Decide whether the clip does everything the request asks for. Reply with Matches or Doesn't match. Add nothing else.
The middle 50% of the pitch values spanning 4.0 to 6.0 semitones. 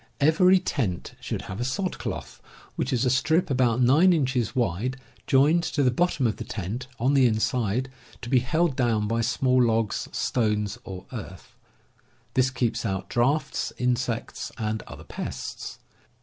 Doesn't match